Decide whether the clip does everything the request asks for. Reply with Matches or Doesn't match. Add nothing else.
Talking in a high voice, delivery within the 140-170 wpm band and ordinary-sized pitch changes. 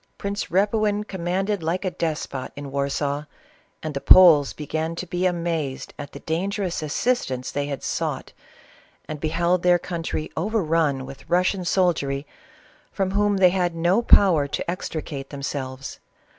Doesn't match